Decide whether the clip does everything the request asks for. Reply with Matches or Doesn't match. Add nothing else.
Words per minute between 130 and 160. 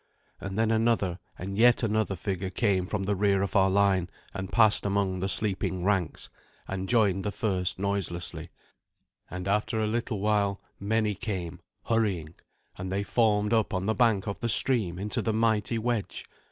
Doesn't match